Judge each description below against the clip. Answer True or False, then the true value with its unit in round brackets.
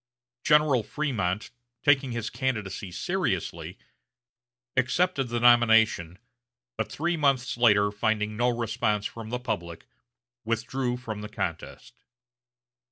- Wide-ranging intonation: False (3.7 semitones)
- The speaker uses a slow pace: True (105 wpm)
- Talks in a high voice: False (120 Hz)